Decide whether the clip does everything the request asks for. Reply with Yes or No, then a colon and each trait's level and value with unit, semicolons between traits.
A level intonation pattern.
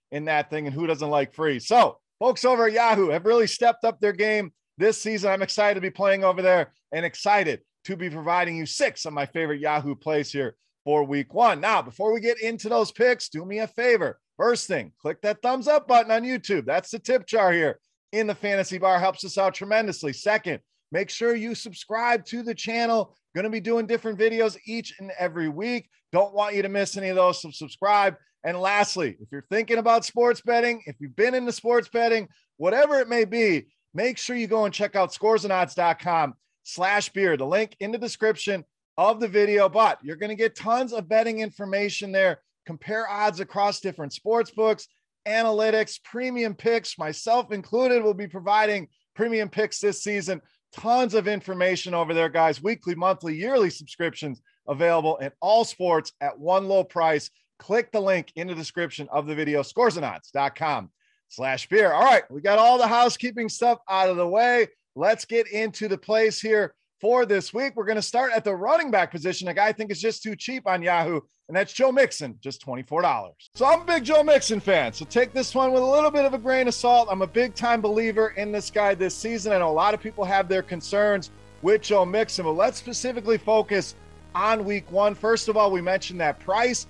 No: average, 4.5 semitones